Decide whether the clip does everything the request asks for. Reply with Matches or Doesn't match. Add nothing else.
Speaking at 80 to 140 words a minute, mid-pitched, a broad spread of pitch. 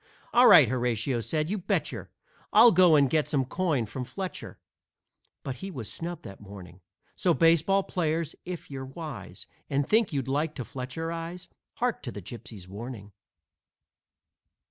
Doesn't match